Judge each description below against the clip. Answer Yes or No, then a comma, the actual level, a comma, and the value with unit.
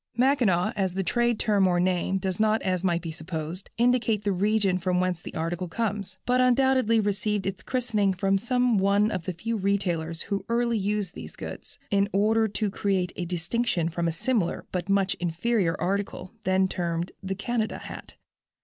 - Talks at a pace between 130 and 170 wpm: No, average, 180 wpm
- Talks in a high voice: Yes, high, 195 Hz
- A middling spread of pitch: Yes, average, 3.4 semitones